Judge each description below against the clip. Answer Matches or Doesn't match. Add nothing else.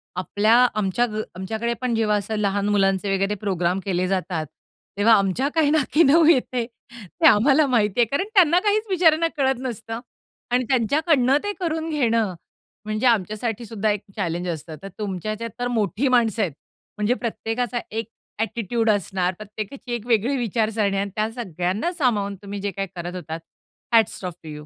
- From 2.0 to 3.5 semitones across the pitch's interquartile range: Doesn't match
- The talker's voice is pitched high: Matches